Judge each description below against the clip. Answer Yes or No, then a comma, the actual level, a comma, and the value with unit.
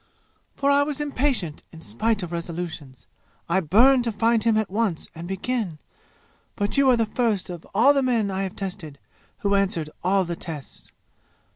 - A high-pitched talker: Yes, high, 200 Hz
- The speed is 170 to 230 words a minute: Yes, average, 175 wpm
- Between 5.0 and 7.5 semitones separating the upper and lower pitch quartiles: Yes, wide, 5.5 semitones